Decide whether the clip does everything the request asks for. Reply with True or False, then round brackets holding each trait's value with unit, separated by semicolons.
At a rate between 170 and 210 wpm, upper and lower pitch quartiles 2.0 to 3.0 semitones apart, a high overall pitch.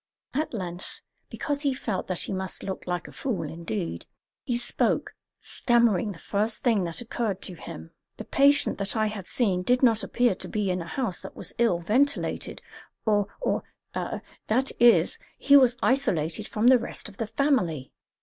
False (180 wpm; 5.2 semitones; 215 Hz)